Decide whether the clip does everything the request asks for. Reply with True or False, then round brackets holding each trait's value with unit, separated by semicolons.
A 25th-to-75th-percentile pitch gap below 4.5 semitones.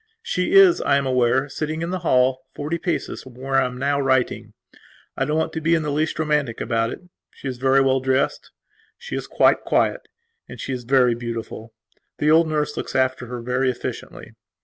True (3.4 semitones)